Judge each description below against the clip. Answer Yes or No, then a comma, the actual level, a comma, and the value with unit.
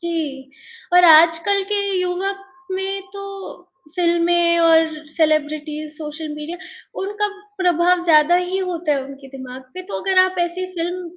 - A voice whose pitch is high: Yes, very high, 340 Hz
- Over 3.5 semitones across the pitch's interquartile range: No, average, 3.0 semitones